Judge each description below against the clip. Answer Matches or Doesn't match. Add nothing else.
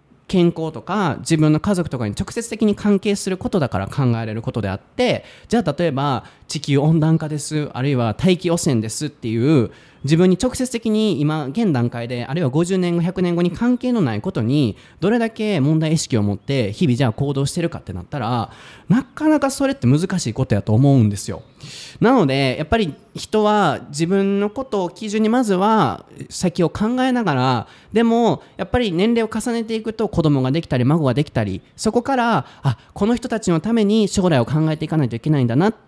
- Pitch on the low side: Doesn't match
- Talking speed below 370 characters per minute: Doesn't match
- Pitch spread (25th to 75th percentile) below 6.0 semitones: Doesn't match